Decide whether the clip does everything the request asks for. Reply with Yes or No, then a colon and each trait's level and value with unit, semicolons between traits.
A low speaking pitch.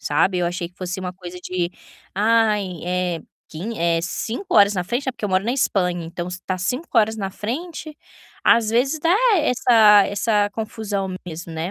No: high, 200 Hz